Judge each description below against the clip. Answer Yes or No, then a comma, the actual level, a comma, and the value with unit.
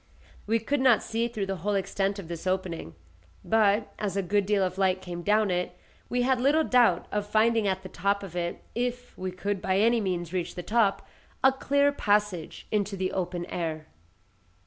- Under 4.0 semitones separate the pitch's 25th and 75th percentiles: Yes, average, 3.4 semitones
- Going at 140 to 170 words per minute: No, average, 195 wpm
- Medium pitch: No, high, 200 Hz